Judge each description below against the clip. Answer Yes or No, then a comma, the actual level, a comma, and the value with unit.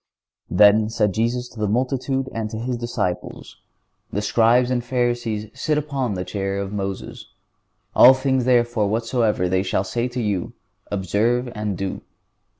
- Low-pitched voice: Yes, low, 115 Hz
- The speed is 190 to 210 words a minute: No, average, 155 wpm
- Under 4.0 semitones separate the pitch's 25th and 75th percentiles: Yes, average, 3.3 semitones